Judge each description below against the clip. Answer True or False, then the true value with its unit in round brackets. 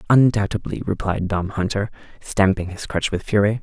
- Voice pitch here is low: True (100 Hz)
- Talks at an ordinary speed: True (150 wpm)